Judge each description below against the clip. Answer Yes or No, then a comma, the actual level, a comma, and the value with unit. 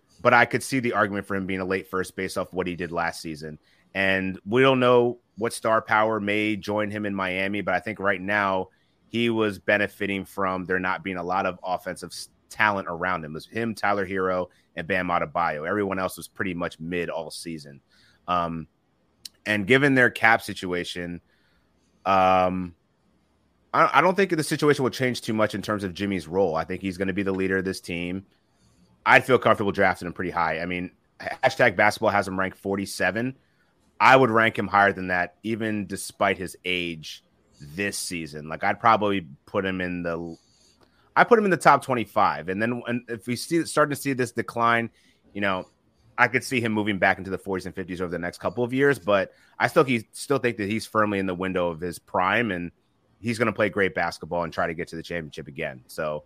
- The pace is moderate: No, fast, 215 wpm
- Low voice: Yes, low, 100 Hz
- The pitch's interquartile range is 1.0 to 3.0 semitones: No, average, 3.8 semitones